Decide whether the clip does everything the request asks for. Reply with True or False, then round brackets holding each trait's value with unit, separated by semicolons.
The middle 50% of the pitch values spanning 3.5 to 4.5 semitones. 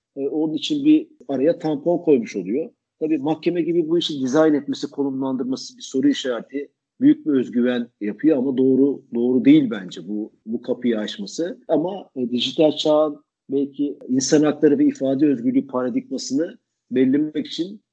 True (4.0 semitones)